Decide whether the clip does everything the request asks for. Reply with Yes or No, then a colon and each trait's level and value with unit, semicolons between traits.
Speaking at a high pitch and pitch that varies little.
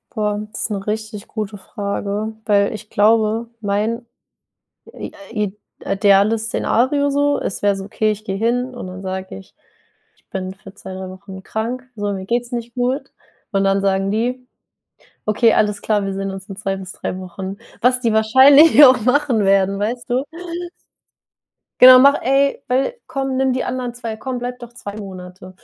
No: high, 215 Hz; average, 4.0 semitones